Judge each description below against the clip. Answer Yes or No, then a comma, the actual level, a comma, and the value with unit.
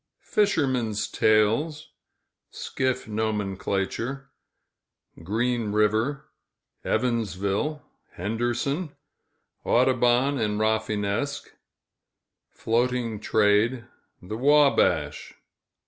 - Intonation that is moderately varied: Yes, average, 3.8 semitones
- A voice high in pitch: No, low, 115 Hz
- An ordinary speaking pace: No, slow, 55 wpm